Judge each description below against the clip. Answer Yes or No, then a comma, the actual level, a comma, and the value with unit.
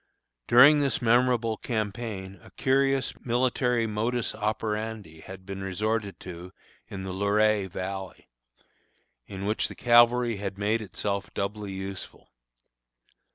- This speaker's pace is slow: Yes, slow, 115 wpm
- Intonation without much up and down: No, average, 3.4 semitones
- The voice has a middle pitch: No, low, 105 Hz